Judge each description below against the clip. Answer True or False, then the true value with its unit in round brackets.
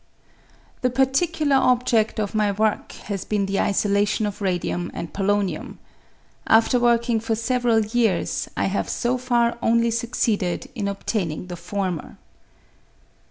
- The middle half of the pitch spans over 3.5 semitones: False (3.2 semitones)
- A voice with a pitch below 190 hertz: False (215 Hz)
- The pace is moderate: False (130 wpm)